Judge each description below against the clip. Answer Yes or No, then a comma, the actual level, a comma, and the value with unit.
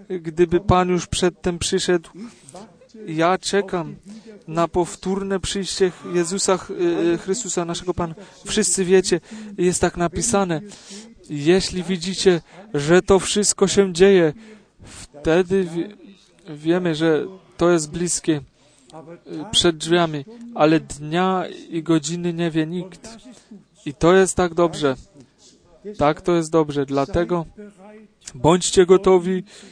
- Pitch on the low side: No, medium, 180 Hz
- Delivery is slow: Yes, slow, 105 wpm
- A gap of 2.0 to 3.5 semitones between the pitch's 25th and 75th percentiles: Yes, narrow, 2.6 semitones